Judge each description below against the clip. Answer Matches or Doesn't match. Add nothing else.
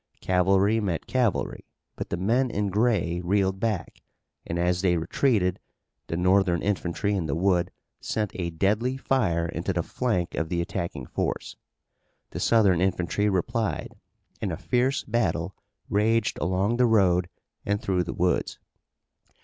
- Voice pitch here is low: Matches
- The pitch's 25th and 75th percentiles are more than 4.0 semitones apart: Doesn't match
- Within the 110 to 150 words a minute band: Matches